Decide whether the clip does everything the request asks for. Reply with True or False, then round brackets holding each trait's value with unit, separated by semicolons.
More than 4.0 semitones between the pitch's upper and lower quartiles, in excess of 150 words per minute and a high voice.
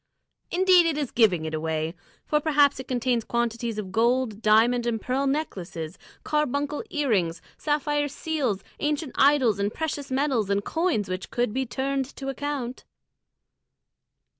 False (5.3 semitones; 140 wpm; 255 Hz)